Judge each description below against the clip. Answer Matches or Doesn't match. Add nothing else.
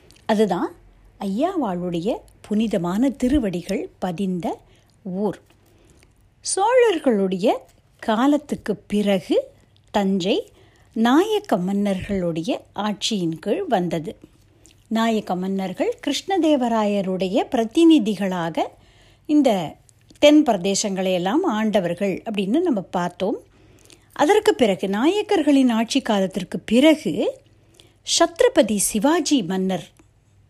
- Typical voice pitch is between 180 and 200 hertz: Doesn't match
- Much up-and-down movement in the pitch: Matches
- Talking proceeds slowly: Matches